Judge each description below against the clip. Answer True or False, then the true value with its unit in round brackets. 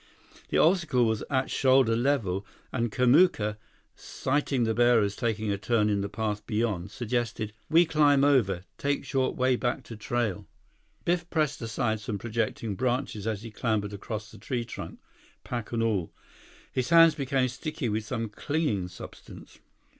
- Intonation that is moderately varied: True (3.9 semitones)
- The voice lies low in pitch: True (120 Hz)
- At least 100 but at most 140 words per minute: False (155 wpm)